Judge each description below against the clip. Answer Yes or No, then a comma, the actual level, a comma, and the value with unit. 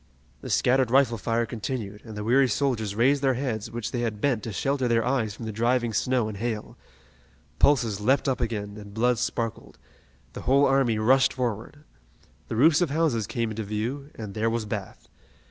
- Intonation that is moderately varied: Yes, average, 3.4 semitones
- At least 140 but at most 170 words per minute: No, average, 190 wpm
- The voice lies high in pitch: No, low, 115 Hz